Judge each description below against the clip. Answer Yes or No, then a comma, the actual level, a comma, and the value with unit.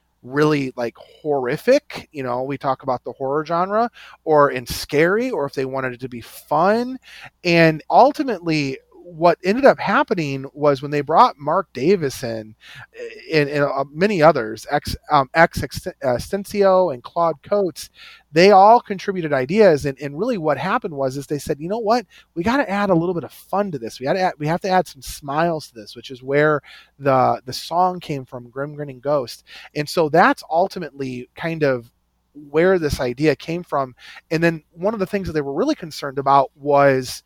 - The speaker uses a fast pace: No, average, 190 wpm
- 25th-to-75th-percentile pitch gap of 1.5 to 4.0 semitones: No, wide, 5.5 semitones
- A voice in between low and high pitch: Yes, medium, 150 Hz